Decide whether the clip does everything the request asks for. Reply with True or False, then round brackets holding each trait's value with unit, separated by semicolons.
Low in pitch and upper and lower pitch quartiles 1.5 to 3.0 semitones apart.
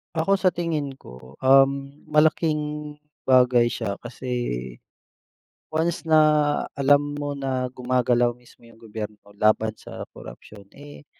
False (130 Hz; 3.9 semitones)